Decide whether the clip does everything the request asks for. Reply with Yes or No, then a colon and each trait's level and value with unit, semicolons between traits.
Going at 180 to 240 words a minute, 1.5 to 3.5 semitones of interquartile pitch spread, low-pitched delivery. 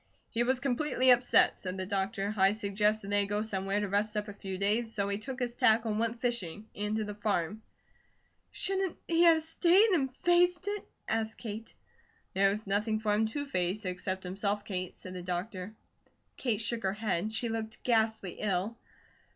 No: average, 190 wpm; average, 3.1 semitones; high, 215 Hz